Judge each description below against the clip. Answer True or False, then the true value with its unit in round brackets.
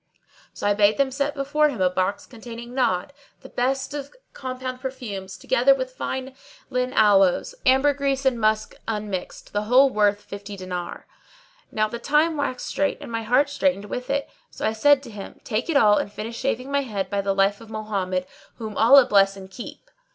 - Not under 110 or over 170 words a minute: False (190 wpm)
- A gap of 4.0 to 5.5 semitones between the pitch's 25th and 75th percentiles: True (5.0 semitones)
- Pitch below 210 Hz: False (235 Hz)